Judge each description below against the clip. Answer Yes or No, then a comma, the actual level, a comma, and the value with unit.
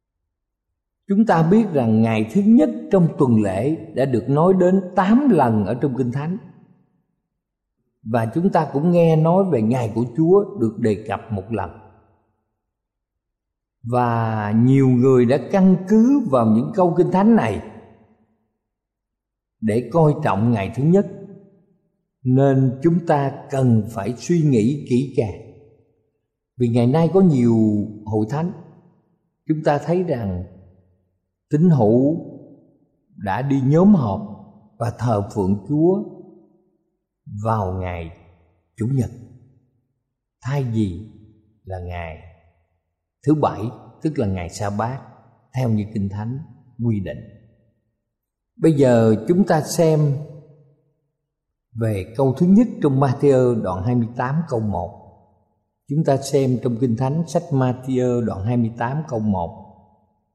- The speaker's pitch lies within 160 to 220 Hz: No, low, 120 Hz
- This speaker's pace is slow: Yes, slow, 130 wpm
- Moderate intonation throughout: No, wide, 6.3 semitones